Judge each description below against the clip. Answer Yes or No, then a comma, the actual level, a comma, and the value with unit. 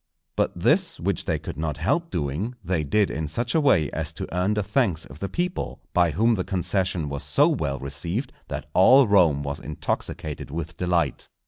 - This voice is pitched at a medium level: No, very low, 90 Hz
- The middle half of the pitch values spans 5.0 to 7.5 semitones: Yes, wide, 5.6 semitones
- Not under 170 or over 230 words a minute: Yes, average, 195 wpm